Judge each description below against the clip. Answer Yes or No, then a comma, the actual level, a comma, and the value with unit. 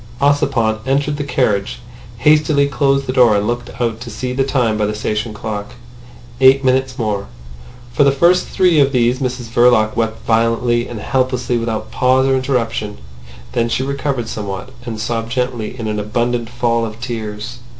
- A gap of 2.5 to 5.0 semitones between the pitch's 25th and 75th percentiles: Yes, average, 3.1 semitones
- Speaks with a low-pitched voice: Yes, low, 120 Hz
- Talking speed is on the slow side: No, average, 170 wpm